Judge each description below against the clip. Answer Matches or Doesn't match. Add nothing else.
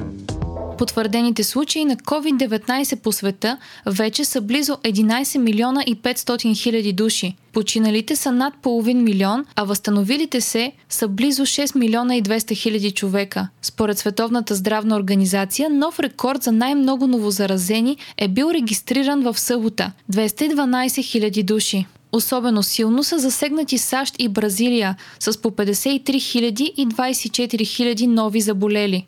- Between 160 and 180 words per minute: Doesn't match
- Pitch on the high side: Matches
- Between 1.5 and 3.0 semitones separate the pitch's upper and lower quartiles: Doesn't match